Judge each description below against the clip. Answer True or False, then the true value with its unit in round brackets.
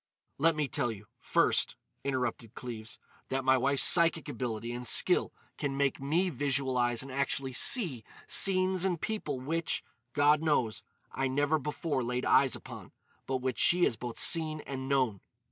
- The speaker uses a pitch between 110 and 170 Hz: True (135 Hz)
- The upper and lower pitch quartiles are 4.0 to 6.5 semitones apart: False (3.5 semitones)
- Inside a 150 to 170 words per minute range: True (160 wpm)